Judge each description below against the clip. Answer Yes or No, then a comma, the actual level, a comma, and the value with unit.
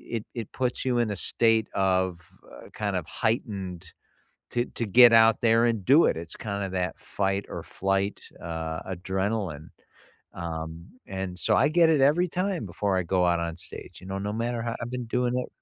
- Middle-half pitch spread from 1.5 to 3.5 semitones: No, average, 4.5 semitones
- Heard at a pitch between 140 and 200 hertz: No, low, 100 Hz